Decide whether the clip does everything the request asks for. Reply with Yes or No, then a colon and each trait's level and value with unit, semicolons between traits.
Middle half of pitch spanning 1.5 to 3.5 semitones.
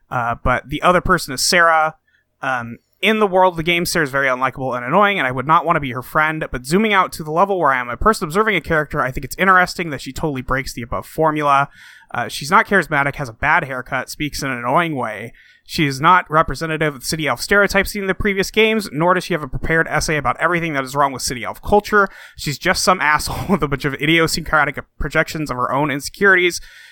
No: average, 4.9 semitones